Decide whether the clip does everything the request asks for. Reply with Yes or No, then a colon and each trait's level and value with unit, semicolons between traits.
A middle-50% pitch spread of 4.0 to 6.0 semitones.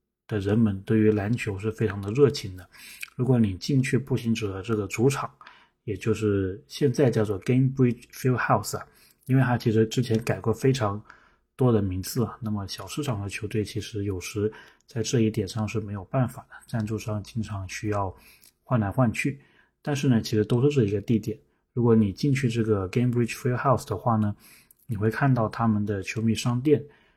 No: average, 3.2 semitones